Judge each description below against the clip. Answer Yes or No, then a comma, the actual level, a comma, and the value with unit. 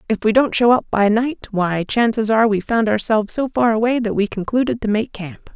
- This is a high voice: Yes, high, 220 Hz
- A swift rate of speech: Yes, fast, 240 wpm